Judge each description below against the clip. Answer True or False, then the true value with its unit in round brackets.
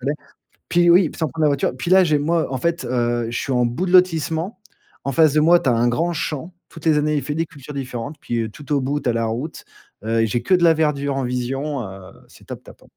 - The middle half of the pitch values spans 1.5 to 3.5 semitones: False (4.9 semitones)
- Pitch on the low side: False (145 Hz)